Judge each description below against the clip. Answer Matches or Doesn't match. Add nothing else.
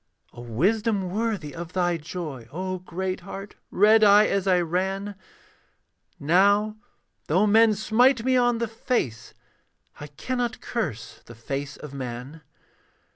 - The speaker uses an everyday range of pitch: Doesn't match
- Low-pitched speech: Doesn't match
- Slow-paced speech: Matches